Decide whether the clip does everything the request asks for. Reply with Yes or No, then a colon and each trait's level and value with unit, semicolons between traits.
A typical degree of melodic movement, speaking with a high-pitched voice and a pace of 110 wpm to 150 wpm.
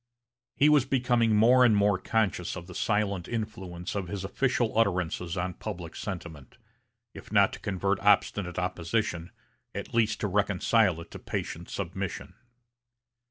No: average, 3.7 semitones; low, 100 Hz; average, 145 wpm